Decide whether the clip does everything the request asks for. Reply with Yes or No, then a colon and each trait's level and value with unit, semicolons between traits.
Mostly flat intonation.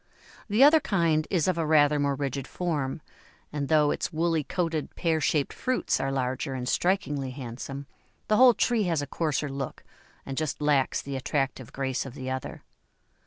No: average, 3.5 semitones